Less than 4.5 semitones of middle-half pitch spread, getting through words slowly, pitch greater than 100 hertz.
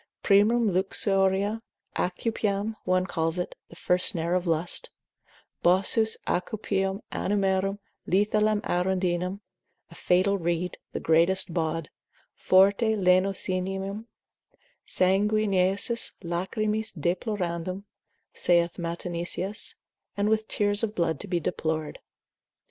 Yes: average, 2.7 semitones; slow, 100 wpm; high, 190 Hz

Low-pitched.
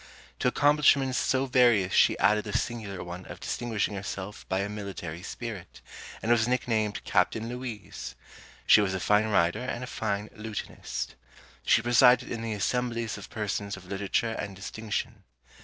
Yes: low, 110 Hz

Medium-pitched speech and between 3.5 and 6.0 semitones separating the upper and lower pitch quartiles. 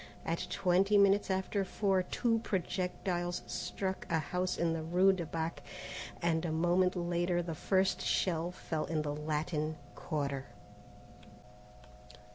No: medium, 175 Hz; average, 2.7 semitones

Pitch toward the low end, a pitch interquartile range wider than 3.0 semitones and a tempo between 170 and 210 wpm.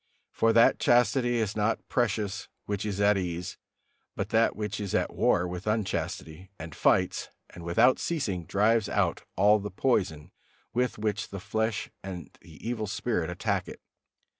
No: low, 105 Hz; average, 3.6 semitones; average, 160 wpm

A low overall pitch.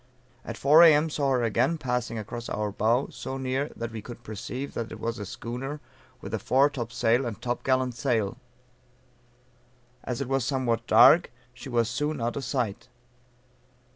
Yes: low, 125 Hz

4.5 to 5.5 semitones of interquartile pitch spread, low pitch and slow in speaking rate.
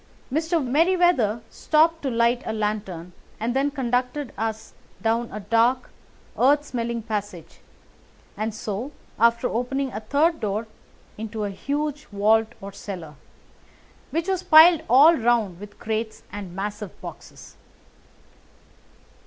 No: average, 5.1 semitones; high, 230 Hz; slow, 125 wpm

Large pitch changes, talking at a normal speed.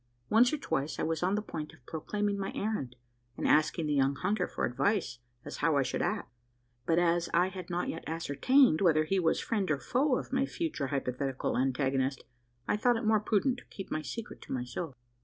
No: wide, 6.9 semitones; fast, 210 wpm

